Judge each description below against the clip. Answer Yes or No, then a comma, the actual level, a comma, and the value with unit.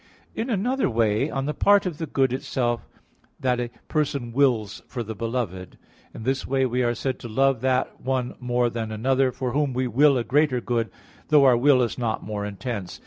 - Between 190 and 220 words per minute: Yes, average, 200 wpm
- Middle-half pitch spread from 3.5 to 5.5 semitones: No, average, 2.7 semitones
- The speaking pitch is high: No, low, 125 Hz